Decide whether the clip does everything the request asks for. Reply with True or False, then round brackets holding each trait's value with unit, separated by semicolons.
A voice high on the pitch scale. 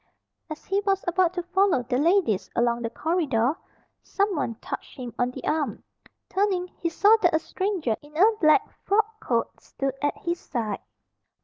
True (330 Hz)